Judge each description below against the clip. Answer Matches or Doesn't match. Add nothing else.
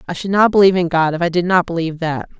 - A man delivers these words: Doesn't match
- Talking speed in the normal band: Doesn't match